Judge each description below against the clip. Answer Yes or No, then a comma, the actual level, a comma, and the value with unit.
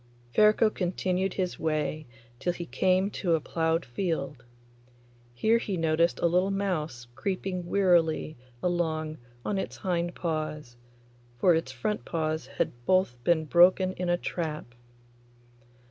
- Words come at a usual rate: No, slow, 130 wpm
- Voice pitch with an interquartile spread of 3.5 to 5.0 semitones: No, average, 3.0 semitones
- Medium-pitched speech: Yes, medium, 170 Hz